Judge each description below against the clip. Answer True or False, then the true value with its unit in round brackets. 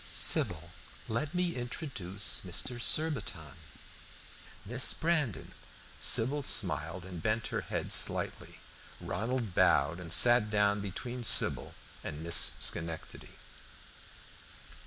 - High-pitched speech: False (105 Hz)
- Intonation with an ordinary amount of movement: False (6.3 semitones)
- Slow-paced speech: True (100 wpm)